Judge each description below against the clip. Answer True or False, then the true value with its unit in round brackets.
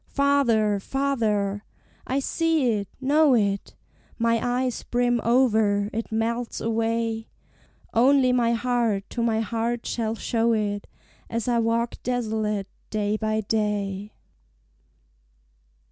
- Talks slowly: True (115 wpm)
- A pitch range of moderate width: False (2.3 semitones)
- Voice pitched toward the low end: False (230 Hz)